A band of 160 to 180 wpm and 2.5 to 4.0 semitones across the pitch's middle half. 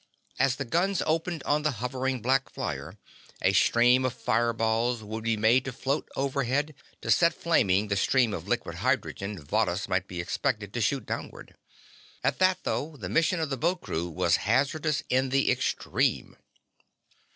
No: average, 170 wpm; average, 4.4 semitones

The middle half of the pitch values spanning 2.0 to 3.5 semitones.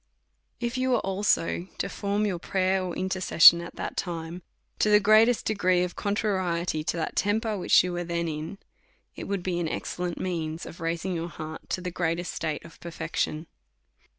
Yes: average, 2.9 semitones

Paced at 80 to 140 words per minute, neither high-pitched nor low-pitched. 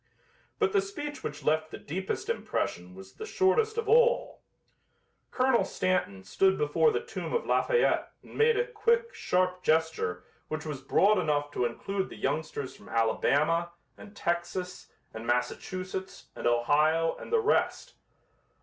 No: average, 150 wpm; medium, 180 Hz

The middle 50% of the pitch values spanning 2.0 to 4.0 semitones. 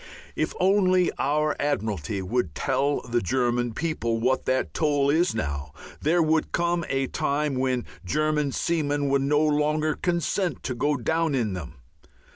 No: average, 4.4 semitones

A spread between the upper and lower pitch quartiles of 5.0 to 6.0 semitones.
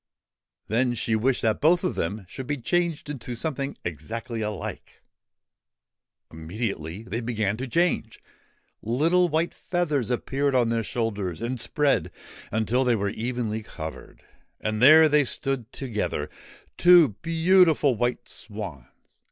Yes: average, 5.3 semitones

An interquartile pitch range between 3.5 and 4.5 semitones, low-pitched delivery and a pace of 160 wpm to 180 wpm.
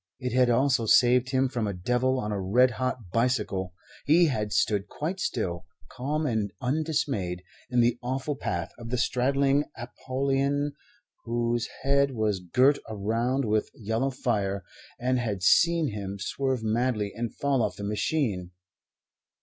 No: average, 4.2 semitones; low, 120 Hz; average, 150 wpm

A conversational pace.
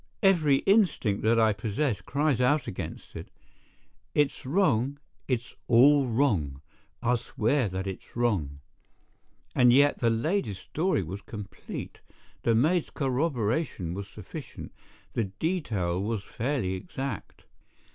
No: slow, 115 wpm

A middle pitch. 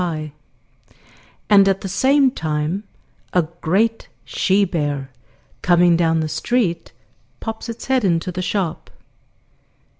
Yes: medium, 180 Hz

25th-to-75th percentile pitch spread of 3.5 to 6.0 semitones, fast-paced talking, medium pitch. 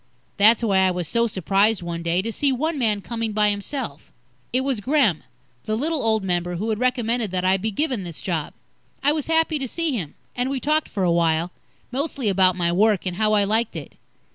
No: wide, 5.4 semitones; fast, 220 wpm; high, 215 Hz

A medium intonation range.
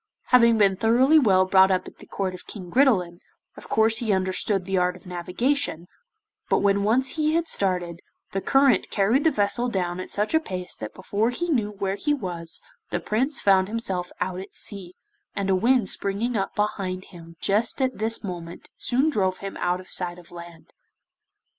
Yes: average, 4.2 semitones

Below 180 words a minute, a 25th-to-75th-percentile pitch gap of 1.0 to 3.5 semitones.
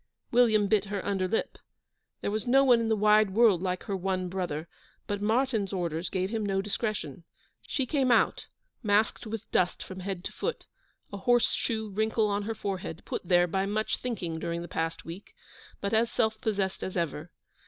No: average, 190 wpm; average, 3.2 semitones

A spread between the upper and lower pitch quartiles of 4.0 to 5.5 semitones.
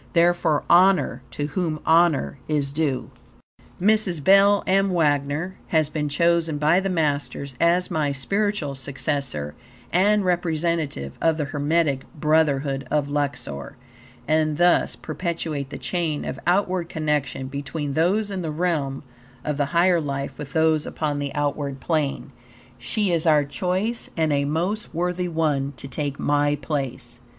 No: average, 3.5 semitones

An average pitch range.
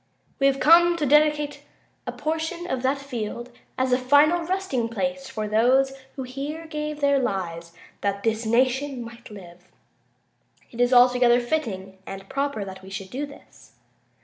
Yes: average, 4.6 semitones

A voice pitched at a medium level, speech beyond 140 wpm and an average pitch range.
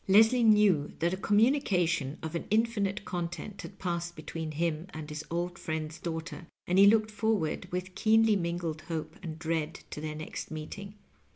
Yes: medium, 175 Hz; average, 170 wpm; average, 4.2 semitones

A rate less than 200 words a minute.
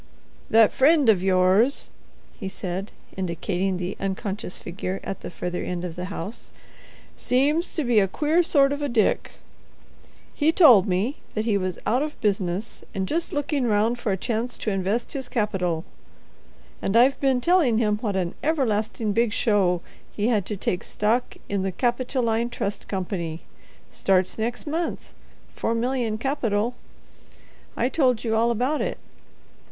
Yes: average, 150 wpm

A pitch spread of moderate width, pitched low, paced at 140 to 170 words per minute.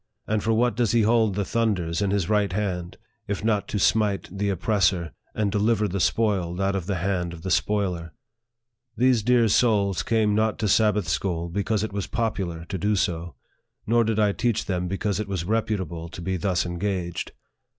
No: average, 3.4 semitones; low, 100 Hz; average, 195 wpm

